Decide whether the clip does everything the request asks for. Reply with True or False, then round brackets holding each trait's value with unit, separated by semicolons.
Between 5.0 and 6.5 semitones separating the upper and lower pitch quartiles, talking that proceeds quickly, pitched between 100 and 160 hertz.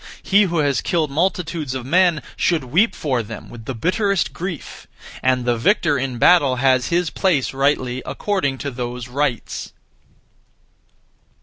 False (5.4 semitones; 145 wpm; 140 Hz)